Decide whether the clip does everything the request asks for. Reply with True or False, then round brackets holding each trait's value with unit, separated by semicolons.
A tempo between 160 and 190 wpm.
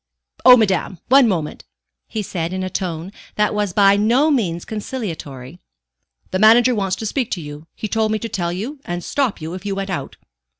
False (200 wpm)